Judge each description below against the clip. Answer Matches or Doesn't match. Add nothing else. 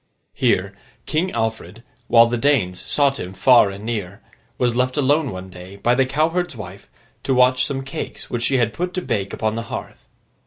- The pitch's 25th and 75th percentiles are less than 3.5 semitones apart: Doesn't match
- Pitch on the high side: Doesn't match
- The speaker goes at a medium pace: Matches